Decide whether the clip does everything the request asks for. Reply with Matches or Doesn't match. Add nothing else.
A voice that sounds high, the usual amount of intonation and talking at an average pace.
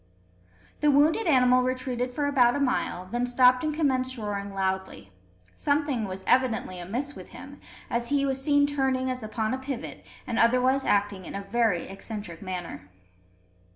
Matches